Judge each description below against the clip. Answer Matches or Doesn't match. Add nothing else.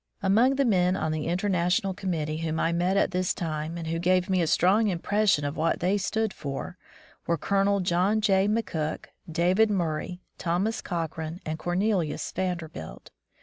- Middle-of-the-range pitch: Matches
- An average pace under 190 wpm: Matches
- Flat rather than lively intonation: Doesn't match